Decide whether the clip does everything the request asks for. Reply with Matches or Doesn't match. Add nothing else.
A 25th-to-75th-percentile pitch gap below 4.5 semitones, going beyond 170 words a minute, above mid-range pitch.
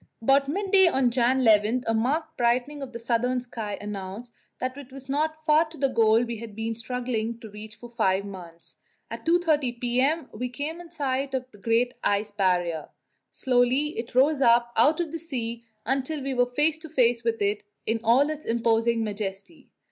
Matches